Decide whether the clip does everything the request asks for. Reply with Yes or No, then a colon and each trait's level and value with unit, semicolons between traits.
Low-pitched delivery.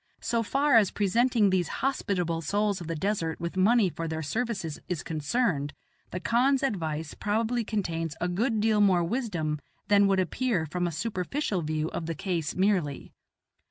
No: high, 190 Hz